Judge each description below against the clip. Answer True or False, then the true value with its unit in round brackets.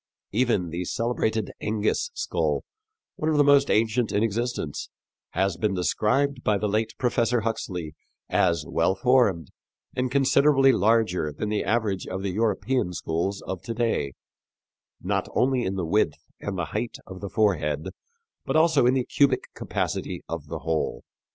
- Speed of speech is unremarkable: True (155 wpm)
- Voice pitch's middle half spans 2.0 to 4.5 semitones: False (5.1 semitones)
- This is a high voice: False (110 Hz)